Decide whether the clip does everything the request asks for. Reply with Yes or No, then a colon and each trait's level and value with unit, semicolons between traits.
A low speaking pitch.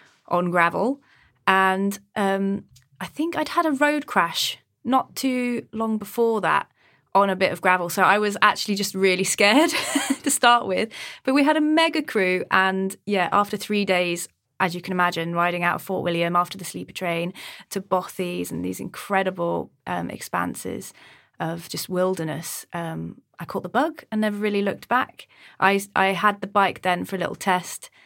No: high, 195 Hz